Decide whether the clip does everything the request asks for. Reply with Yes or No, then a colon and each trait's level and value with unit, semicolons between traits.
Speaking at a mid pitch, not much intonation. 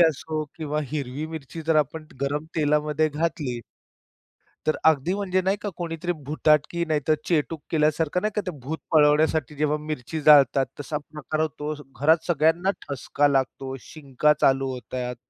Yes: medium, 155 Hz; narrow, 2.0 semitones